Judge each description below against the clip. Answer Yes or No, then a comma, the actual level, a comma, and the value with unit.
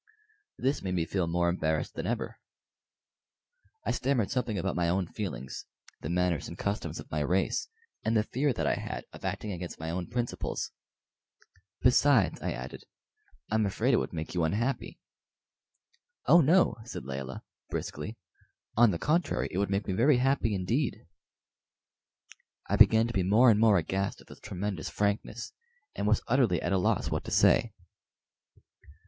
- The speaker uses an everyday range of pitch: Yes, average, 5.0 semitones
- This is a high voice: No, low, 100 Hz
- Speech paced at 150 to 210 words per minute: Yes, average, 165 wpm